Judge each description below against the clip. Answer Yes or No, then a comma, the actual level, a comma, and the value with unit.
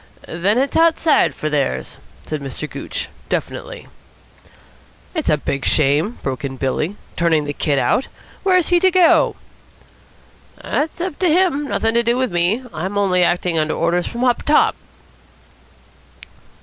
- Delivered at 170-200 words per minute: No, average, 150 wpm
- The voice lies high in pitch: Yes, high, 195 Hz